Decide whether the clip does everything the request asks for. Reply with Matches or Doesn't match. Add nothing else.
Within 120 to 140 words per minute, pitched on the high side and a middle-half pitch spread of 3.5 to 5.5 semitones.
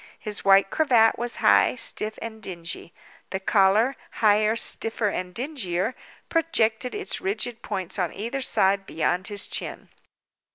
Matches